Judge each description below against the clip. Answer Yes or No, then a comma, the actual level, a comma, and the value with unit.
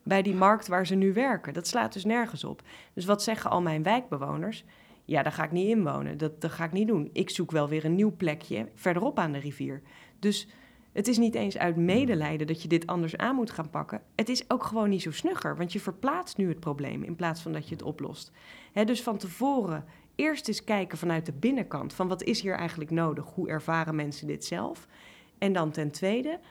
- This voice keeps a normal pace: No, fast, 230 wpm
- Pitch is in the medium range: Yes, medium, 180 Hz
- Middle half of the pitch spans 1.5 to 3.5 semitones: No, wide, 5.6 semitones